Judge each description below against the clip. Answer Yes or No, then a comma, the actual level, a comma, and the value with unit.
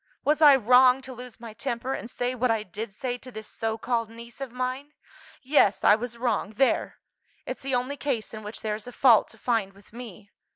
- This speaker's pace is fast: Yes, fast, 220 wpm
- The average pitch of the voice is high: Yes, high, 240 Hz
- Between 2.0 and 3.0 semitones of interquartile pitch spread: Yes, average, 2.7 semitones